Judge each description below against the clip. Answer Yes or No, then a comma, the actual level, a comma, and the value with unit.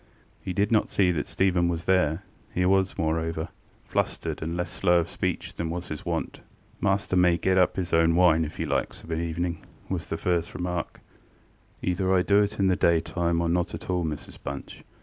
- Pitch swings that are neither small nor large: No, narrow, 1.9 semitones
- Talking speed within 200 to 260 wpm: Yes, fast, 205 wpm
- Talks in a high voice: No, very low, 85 Hz